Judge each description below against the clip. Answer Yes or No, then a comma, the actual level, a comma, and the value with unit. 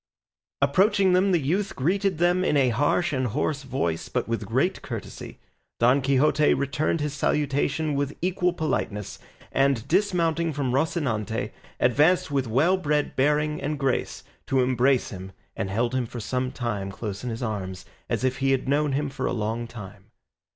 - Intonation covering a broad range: No, average, 4.3 semitones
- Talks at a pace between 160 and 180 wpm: Yes, average, 170 wpm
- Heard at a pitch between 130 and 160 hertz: Yes, medium, 140 Hz